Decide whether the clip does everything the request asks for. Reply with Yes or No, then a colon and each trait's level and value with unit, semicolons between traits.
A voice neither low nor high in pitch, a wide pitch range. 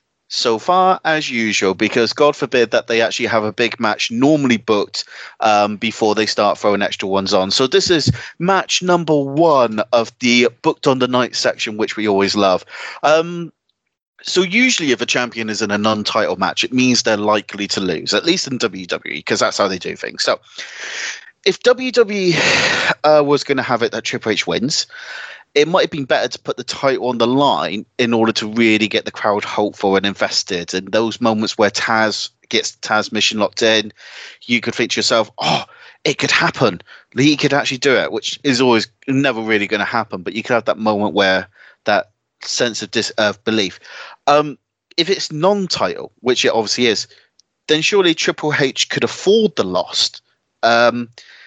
No: low, 125 Hz; wide, 6.7 semitones